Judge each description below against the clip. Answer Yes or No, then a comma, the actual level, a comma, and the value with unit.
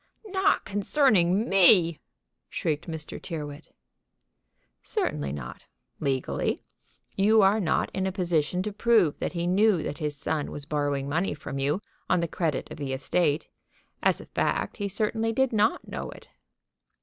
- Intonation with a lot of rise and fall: Yes, wide, 5.8 semitones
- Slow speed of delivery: No, average, 150 wpm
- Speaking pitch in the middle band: Yes, medium, 175 Hz